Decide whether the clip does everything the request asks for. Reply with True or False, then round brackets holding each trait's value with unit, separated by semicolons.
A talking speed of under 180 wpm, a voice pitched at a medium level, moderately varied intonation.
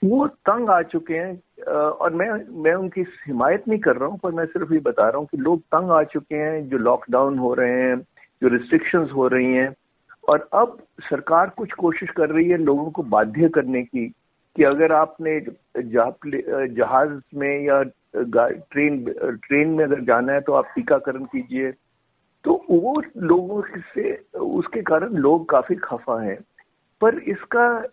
False (170 wpm; 160 Hz; 6.2 semitones)